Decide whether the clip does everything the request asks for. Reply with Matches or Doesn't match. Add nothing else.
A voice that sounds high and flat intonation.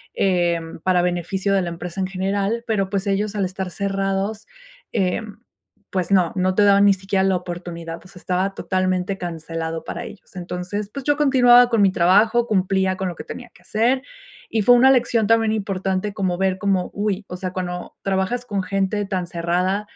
Matches